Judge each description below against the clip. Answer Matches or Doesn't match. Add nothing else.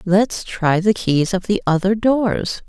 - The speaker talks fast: Doesn't match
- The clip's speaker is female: Matches